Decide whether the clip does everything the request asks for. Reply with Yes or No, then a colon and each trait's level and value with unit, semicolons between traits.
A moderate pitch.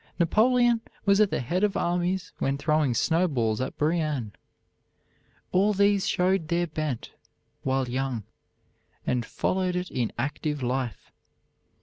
Yes: medium, 160 Hz